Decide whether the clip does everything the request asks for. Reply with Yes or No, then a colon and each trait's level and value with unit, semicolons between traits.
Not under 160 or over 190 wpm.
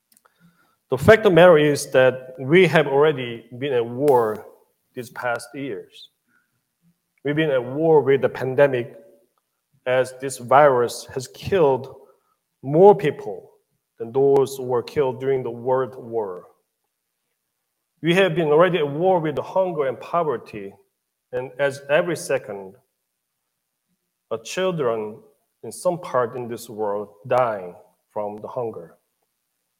No: slow, 135 wpm